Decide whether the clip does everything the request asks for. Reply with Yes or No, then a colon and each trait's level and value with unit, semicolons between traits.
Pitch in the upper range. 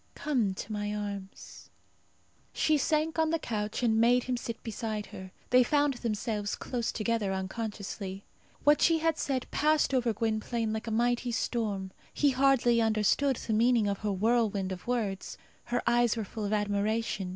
Yes: high, 225 Hz